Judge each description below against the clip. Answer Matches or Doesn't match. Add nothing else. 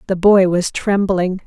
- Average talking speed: Matches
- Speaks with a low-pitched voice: Doesn't match